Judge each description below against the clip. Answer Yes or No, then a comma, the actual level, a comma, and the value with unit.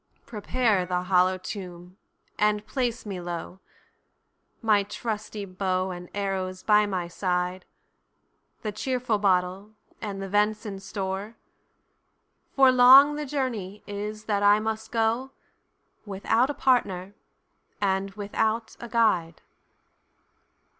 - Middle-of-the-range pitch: No, high, 205 Hz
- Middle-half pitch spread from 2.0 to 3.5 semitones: Yes, average, 3.1 semitones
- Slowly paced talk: Yes, slow, 100 wpm